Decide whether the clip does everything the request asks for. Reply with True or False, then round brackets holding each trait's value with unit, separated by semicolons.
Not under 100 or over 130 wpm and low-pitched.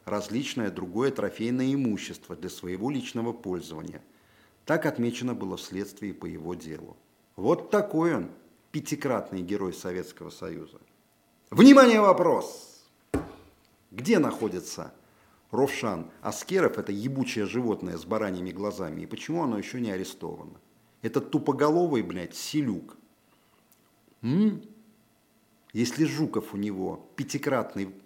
True (110 wpm; 110 Hz)